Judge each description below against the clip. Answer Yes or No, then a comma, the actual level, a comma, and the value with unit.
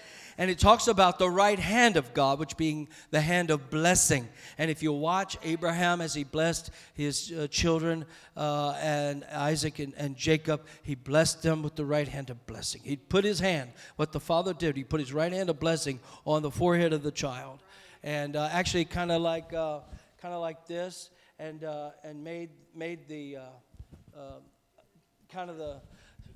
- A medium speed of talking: Yes, average, 190 wpm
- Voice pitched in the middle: Yes, medium, 155 Hz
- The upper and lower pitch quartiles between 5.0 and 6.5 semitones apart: No, narrow, 2.5 semitones